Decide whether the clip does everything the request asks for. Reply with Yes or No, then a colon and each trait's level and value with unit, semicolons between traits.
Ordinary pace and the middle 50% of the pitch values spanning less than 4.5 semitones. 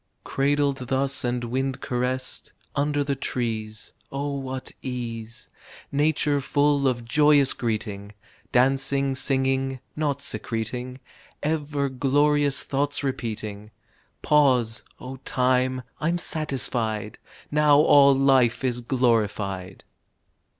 No: slow, 100 wpm; average, 2.8 semitones